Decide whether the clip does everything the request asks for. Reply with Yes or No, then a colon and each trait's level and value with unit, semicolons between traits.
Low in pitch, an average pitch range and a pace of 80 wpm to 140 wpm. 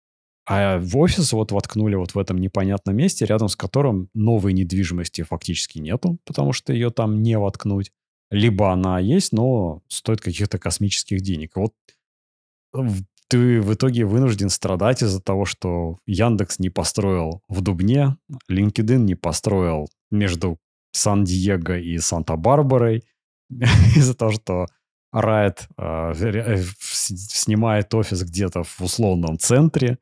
Yes: low, 100 Hz; average, 3.7 semitones; average, 125 wpm